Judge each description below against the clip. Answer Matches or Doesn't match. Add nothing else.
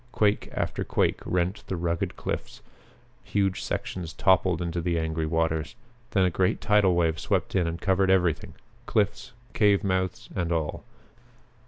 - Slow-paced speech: Doesn't match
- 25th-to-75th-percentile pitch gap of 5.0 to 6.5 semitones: Doesn't match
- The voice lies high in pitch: Doesn't match